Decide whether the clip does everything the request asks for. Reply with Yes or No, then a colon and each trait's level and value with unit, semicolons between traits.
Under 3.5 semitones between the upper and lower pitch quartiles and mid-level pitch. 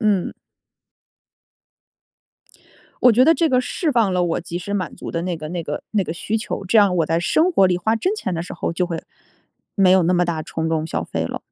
No: average, 4.6 semitones; medium, 180 Hz